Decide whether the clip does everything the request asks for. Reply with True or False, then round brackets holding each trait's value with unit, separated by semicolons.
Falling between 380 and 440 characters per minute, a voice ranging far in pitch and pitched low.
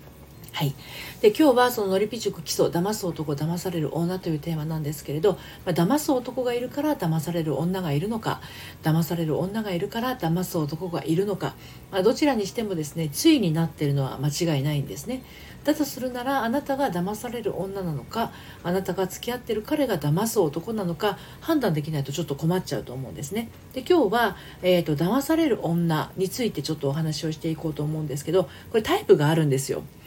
False (425 characters per minute; 6.5 semitones; 180 Hz)